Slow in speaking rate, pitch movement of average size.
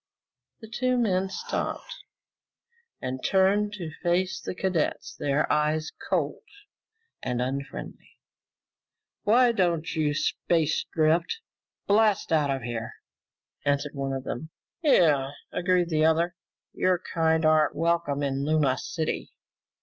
Yes: slow, 120 wpm; average, 4.6 semitones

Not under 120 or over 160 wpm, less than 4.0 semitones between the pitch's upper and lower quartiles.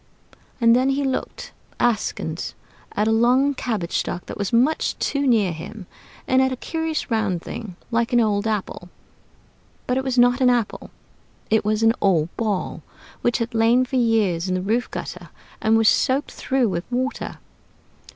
No: average, 170 wpm; average, 3.5 semitones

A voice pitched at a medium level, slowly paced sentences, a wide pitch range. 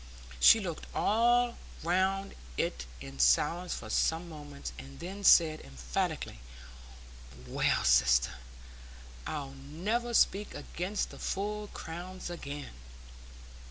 Yes: medium, 165 Hz; slow, 105 wpm; wide, 6.5 semitones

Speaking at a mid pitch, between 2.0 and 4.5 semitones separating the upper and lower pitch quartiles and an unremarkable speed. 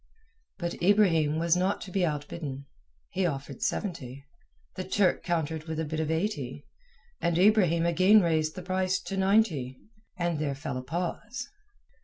Yes: medium, 170 Hz; average, 3.6 semitones; average, 155 wpm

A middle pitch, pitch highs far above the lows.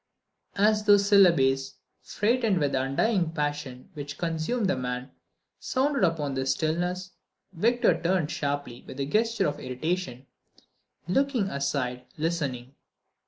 Yes: medium, 160 Hz; wide, 6.6 semitones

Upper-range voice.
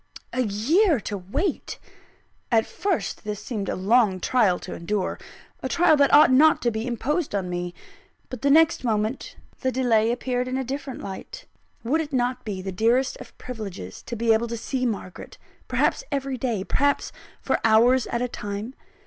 Yes: high, 240 Hz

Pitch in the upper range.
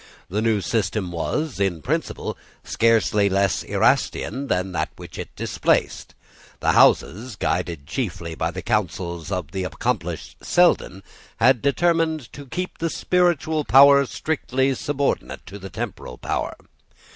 No: low, 110 Hz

